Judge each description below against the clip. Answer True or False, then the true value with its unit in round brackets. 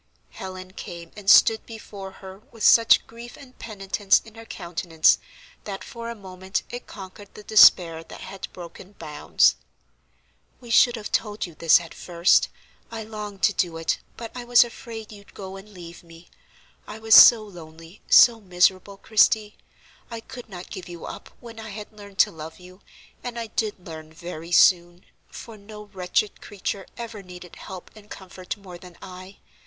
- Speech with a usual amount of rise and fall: True (3.6 semitones)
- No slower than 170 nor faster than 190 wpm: True (175 wpm)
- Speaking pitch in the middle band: False (195 Hz)